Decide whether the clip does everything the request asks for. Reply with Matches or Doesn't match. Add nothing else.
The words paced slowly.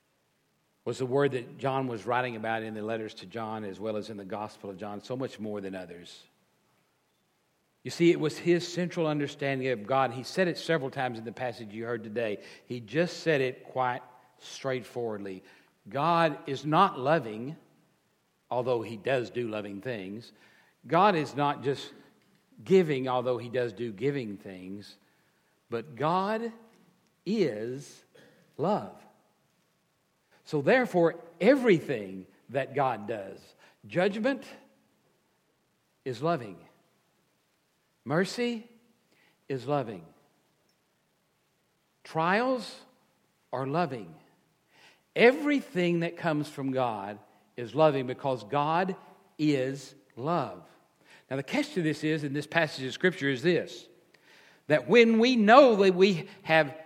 Matches